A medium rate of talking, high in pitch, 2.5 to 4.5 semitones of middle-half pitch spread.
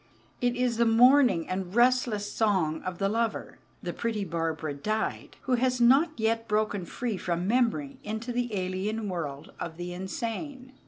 No: average, 160 wpm; high, 220 Hz; average, 4.9 semitones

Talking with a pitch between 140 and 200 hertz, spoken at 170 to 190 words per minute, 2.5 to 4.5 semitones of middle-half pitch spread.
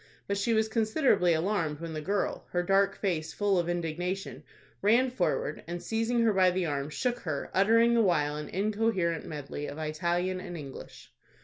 No: medium, 185 Hz; average, 180 wpm; average, 5.0 semitones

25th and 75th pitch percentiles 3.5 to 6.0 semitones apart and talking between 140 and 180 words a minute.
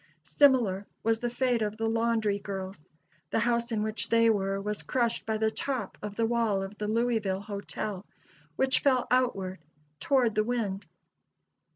No: average, 2.7 semitones; average, 165 wpm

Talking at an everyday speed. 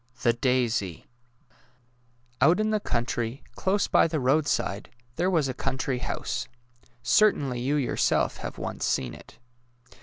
No: slow, 130 wpm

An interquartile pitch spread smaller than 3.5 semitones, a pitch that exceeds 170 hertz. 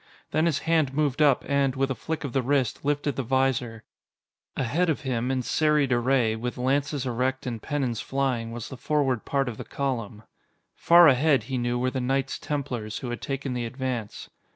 No: narrow, 2.6 semitones; low, 130 Hz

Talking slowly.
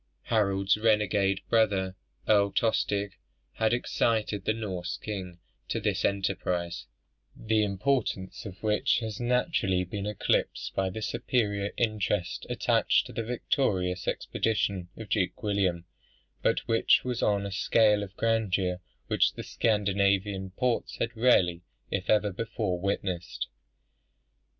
Yes: slow, 125 wpm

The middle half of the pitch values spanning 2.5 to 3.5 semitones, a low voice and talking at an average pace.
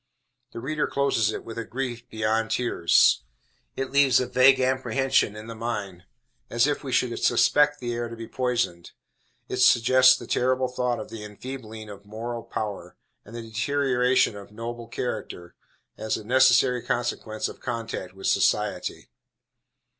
Yes: average, 2.9 semitones; low, 120 Hz; average, 155 wpm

